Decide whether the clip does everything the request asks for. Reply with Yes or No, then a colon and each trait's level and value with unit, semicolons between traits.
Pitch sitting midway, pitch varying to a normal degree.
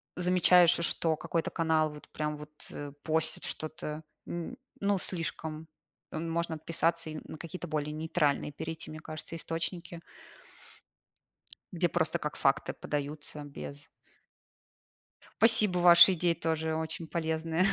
No: medium, 160 Hz; narrow, 1.7 semitones